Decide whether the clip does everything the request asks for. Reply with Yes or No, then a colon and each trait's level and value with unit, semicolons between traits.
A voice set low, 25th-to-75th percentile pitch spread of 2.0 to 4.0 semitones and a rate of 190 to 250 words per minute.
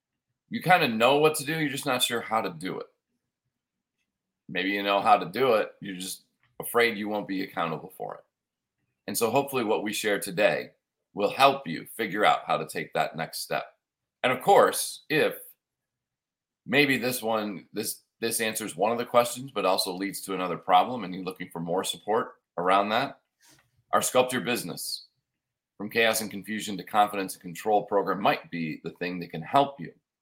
No: low, 110 Hz; average, 4.7 semitones; average, 195 wpm